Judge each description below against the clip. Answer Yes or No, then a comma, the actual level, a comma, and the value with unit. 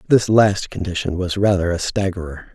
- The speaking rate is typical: Yes, average, 165 wpm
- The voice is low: Yes, very low, 95 Hz